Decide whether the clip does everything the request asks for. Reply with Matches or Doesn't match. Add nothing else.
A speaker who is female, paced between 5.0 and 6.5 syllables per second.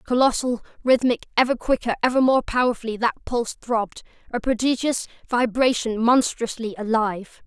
Matches